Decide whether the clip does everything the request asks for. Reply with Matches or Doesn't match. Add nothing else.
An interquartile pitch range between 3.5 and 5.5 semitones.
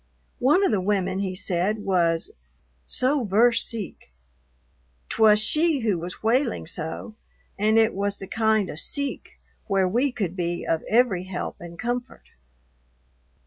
Matches